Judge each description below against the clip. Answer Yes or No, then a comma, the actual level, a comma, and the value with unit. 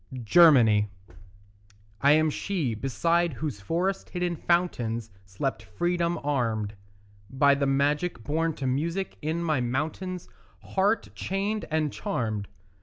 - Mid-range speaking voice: Yes, medium, 150 Hz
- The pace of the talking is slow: Yes, slow, 115 wpm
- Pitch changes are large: Yes, wide, 5.9 semitones